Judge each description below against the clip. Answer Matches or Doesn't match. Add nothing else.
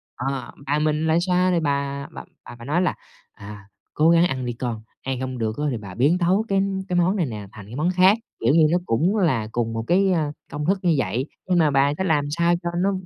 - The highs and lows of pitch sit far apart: Matches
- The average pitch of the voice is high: Doesn't match